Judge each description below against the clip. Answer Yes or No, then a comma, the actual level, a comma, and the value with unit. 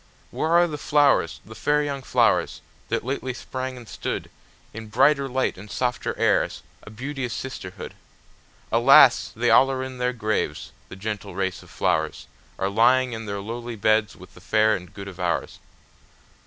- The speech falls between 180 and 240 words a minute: No, average, 160 wpm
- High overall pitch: No, low, 115 Hz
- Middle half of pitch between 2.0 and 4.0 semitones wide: No, average, 4.5 semitones